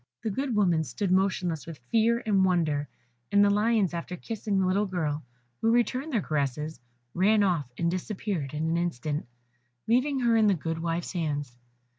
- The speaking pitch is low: No, medium, 185 Hz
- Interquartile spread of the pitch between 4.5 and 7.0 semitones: Yes, average, 5.1 semitones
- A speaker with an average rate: Yes, average, 175 wpm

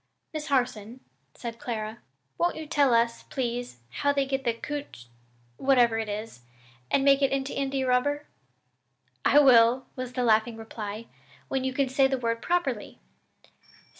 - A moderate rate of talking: Yes, average, 155 wpm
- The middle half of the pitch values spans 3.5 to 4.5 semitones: No, average, 3.0 semitones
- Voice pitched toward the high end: Yes, very high, 250 Hz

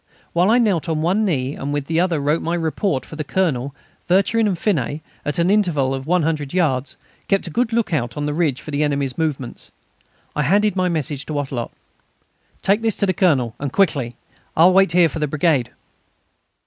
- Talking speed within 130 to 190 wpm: No, fast, 205 wpm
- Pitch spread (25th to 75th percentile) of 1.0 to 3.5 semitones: No, average, 4.6 semitones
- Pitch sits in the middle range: Yes, medium, 160 Hz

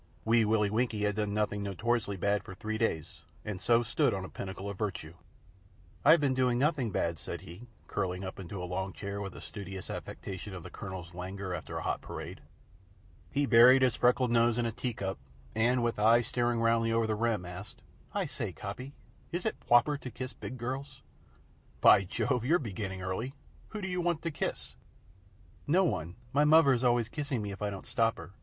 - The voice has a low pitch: Yes, low, 115 Hz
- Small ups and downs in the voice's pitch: No, average, 4.3 semitones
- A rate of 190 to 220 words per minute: Yes, average, 200 wpm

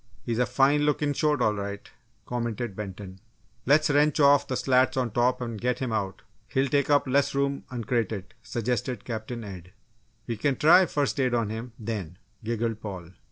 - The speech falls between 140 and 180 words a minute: Yes, average, 175 wpm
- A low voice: Yes, low, 120 Hz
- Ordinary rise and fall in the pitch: Yes, average, 4.3 semitones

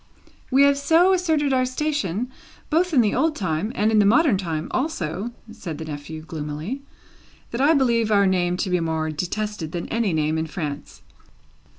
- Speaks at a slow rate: No, average, 180 wpm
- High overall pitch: Yes, high, 205 Hz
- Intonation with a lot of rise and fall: Yes, wide, 8.9 semitones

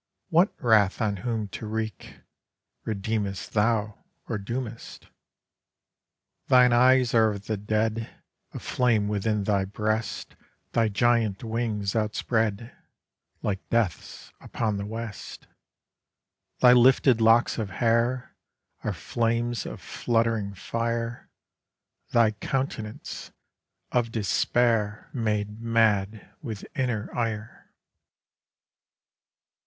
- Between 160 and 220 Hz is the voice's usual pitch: No, low, 110 Hz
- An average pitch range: No, narrow, 2.0 semitones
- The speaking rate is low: Yes, slow, 100 wpm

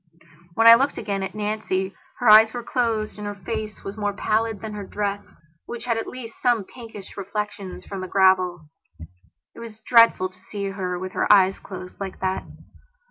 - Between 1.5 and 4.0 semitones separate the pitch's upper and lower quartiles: Yes, average, 2.7 semitones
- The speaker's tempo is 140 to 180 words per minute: No, average, 190 wpm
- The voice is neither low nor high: No, high, 205 Hz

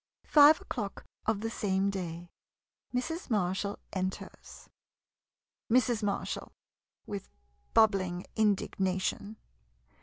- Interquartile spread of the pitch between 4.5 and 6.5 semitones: No, average, 3.0 semitones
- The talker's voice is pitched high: Yes, high, 200 Hz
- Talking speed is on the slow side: Yes, slow, 90 wpm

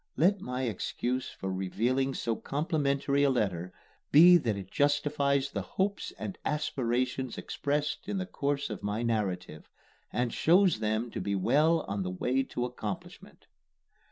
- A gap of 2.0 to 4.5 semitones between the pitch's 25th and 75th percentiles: No, average, 5.2 semitones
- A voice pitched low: Yes, low, 130 Hz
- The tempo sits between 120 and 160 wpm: Yes, average, 150 wpm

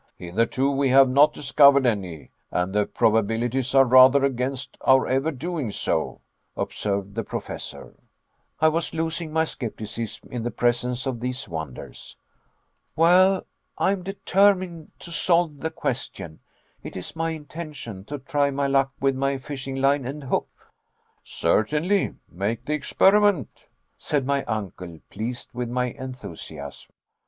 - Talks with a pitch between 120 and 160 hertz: Yes, low, 135 Hz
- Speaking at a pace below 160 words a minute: Yes, average, 140 wpm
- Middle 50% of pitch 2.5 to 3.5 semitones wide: No, average, 4.7 semitones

